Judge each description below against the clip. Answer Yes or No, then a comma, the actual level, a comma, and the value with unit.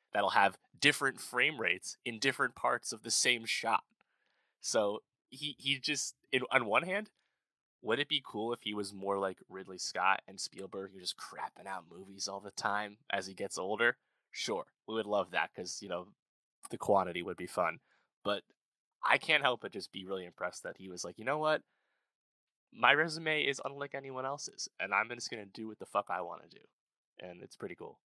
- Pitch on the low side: Yes, low, 110 Hz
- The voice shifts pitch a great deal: Yes, wide, 6.2 semitones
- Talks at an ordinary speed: No, fast, 210 wpm